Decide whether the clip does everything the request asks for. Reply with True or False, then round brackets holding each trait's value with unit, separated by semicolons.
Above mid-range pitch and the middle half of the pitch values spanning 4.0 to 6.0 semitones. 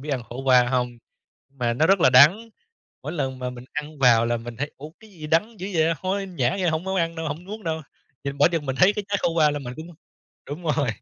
False (150 Hz; 5.2 semitones)